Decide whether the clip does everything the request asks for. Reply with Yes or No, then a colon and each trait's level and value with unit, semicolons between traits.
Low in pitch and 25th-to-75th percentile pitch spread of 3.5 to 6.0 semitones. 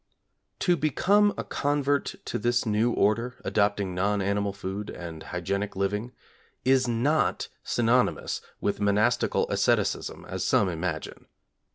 Yes: low, 105 Hz; average, 4.2 semitones